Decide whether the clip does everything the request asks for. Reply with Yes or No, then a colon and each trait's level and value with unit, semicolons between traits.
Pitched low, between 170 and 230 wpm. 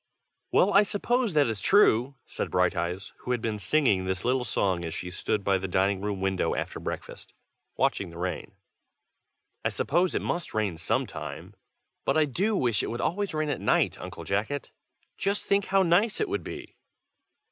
Yes: low, 115 Hz; average, 185 wpm